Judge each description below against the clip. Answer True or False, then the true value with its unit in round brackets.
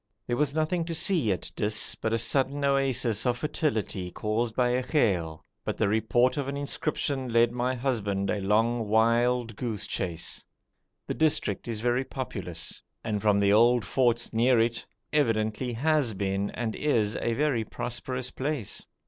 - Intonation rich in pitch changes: False (3.6 semitones)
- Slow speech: False (165 wpm)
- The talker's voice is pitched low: True (120 Hz)